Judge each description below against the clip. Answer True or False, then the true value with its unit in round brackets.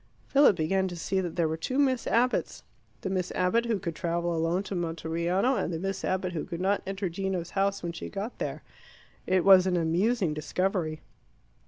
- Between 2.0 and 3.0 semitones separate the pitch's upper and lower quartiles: True (2.6 semitones)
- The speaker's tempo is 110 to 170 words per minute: False (195 wpm)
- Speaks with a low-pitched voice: False (185 Hz)